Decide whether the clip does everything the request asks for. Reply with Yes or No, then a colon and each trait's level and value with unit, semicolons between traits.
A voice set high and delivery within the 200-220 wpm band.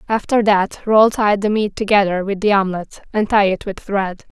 Yes: high, 205 Hz; fast, 205 wpm